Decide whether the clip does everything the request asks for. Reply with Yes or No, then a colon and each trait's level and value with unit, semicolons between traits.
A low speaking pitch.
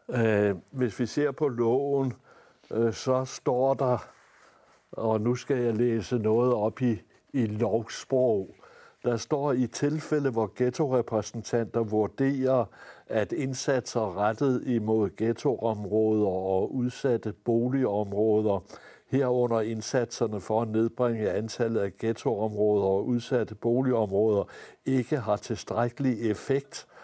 Yes: low, 115 Hz